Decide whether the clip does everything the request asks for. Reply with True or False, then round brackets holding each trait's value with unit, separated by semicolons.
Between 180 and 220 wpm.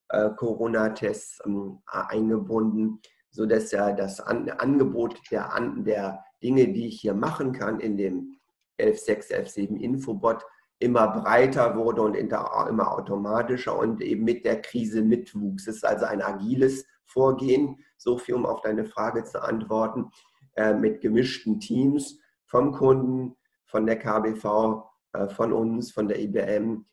False (125 wpm)